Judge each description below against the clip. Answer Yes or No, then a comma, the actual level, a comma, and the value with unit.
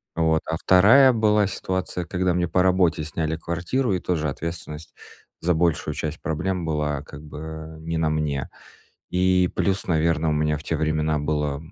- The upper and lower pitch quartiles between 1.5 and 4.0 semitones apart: Yes, average, 2.9 semitones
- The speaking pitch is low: Yes, very low, 80 Hz